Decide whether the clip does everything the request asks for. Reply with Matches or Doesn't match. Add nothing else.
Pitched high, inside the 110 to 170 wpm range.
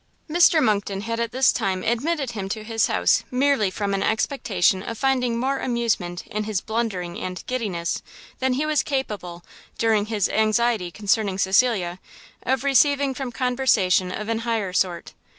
Matches